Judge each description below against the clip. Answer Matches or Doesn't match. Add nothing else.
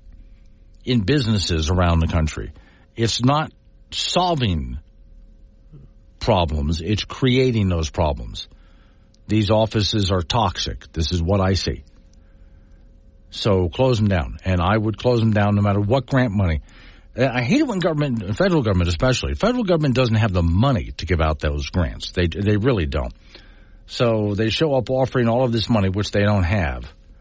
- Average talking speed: Matches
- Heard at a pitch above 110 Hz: Doesn't match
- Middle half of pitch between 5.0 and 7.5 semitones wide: Matches